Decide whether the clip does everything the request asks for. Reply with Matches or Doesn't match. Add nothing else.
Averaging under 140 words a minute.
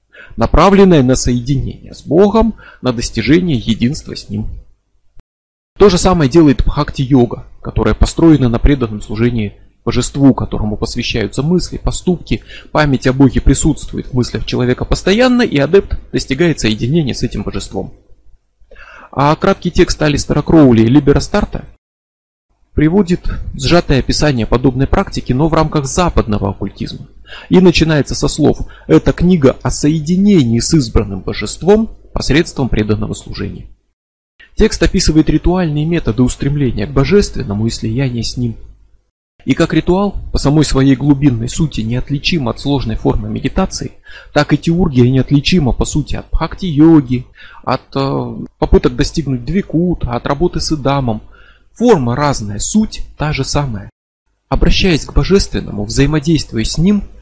Matches